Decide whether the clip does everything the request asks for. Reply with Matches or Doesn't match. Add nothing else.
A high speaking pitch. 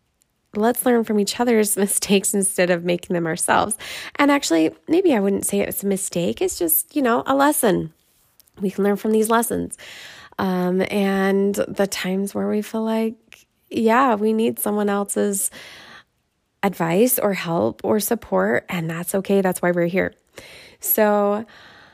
Matches